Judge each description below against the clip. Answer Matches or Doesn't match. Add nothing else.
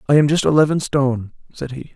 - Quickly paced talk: Matches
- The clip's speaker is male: Matches